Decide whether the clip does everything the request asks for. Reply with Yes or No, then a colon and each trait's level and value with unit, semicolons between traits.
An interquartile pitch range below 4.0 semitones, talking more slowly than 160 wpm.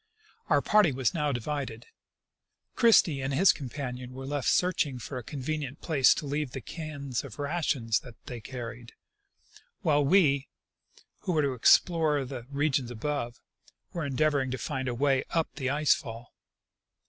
Yes: average, 3.2 semitones; average, 150 wpm